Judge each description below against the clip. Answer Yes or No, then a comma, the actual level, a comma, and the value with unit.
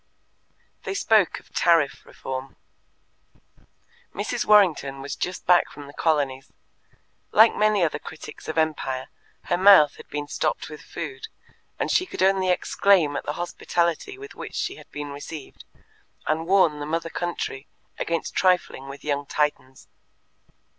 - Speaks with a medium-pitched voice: Yes, medium, 160 Hz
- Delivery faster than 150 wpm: No, average, 145 wpm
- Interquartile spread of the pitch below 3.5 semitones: No, average, 4.3 semitones